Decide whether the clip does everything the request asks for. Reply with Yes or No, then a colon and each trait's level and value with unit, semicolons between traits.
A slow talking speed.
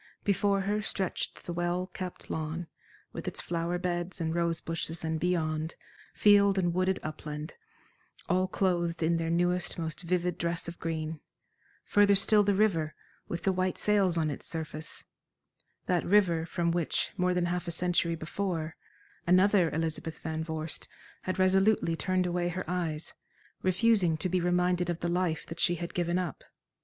No: average, 165 wpm